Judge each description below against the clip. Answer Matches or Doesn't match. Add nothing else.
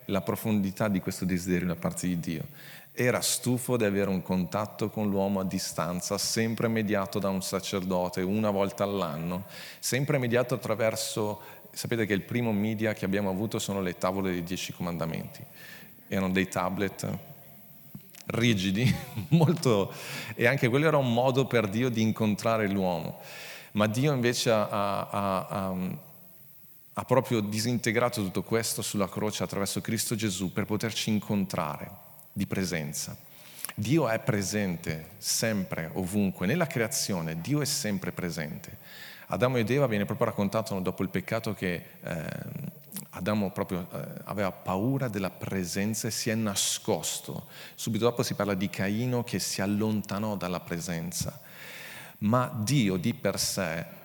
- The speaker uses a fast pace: Doesn't match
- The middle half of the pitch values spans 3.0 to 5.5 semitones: Matches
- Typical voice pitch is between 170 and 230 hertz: Doesn't match